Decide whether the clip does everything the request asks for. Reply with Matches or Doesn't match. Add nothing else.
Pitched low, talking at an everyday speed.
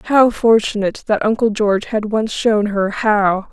Doesn't match